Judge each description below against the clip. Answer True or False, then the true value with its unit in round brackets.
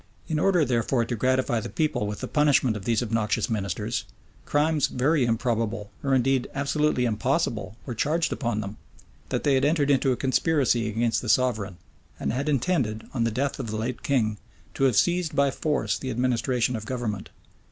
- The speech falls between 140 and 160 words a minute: False (185 wpm)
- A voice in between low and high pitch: False (125 Hz)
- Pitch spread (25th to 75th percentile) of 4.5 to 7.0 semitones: False (3.9 semitones)